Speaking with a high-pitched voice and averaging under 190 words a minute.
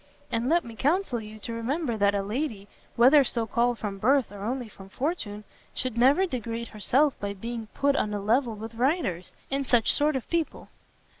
No: high, 235 Hz; average, 195 wpm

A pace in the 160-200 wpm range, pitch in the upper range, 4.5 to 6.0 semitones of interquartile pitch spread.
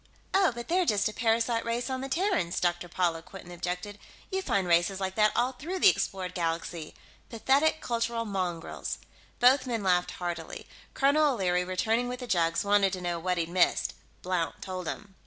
Yes: average, 180 wpm; high, 200 Hz; wide, 5.6 semitones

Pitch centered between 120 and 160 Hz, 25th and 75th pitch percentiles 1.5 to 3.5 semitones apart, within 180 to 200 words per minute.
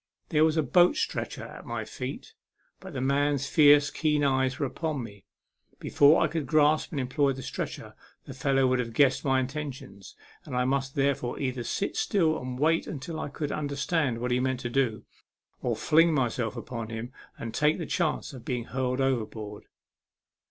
Yes: low, 135 Hz; average, 3.1 semitones; average, 185 wpm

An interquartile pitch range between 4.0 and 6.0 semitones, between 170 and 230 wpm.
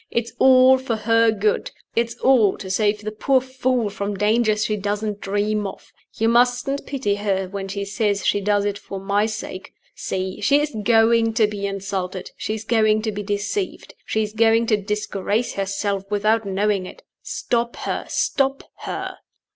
No: narrow, 2.4 semitones; average, 175 wpm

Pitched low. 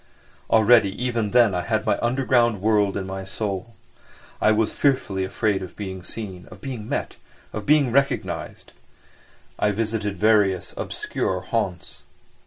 Yes: low, 110 Hz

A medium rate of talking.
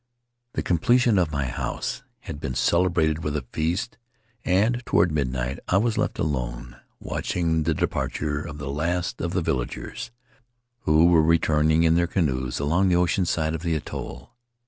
Yes: average, 165 wpm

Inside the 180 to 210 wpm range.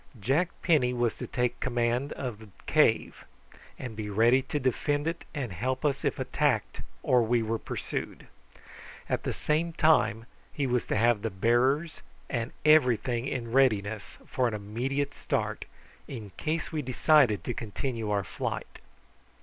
No: average, 155 wpm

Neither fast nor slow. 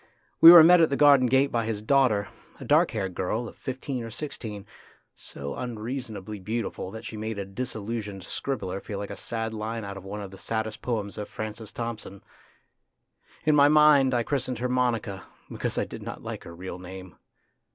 Yes: average, 195 wpm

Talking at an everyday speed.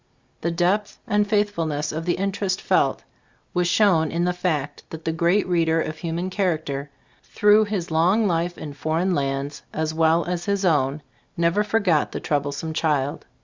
Yes: average, 165 wpm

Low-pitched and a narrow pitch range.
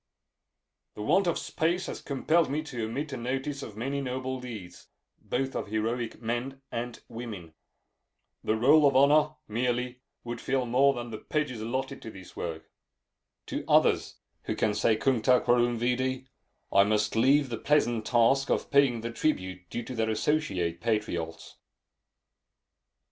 No: low, 120 Hz; average, 3.6 semitones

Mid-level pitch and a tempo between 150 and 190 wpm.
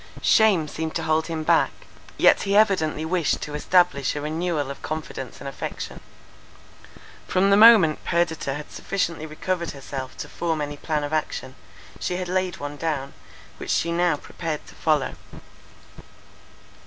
Yes: medium, 160 Hz; average, 155 wpm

